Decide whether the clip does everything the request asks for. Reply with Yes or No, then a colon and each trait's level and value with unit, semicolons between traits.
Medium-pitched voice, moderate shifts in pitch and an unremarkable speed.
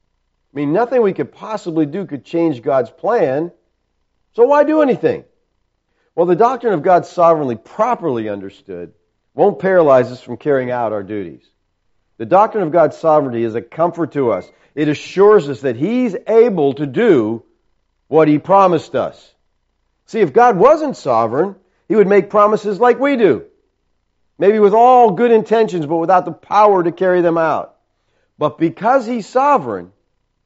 No: medium, 170 Hz; wide, 8.1 semitones; average, 160 wpm